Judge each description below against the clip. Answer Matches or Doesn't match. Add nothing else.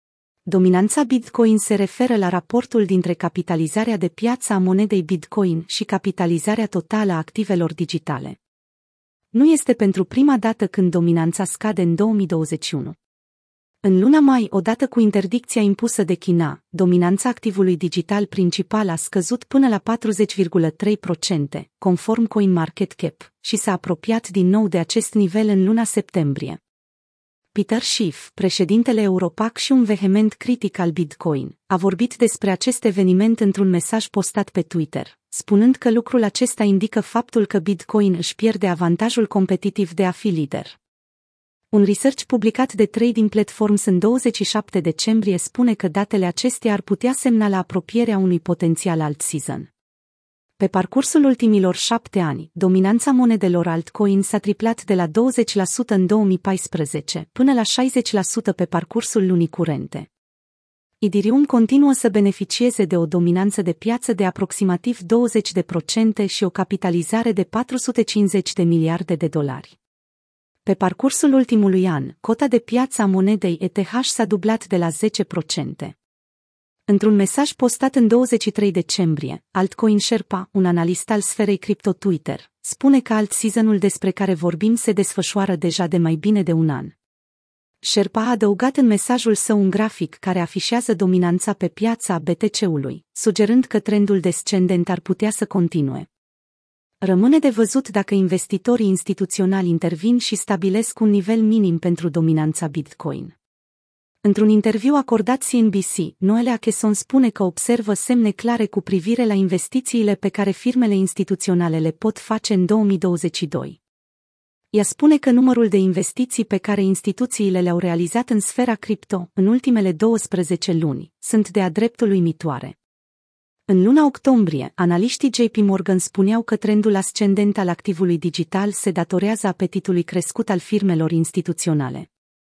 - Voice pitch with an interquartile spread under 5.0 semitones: Matches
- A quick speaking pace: Doesn't match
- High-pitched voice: Matches